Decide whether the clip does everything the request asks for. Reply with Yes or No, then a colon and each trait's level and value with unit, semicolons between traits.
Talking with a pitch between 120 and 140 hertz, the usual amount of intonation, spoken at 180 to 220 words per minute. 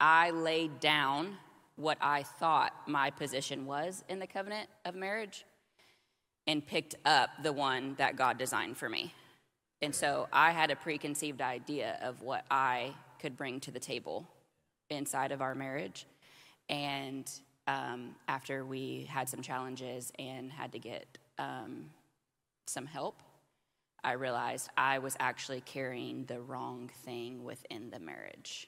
No: low, 135 Hz; average, 3.0 semitones; average, 145 wpm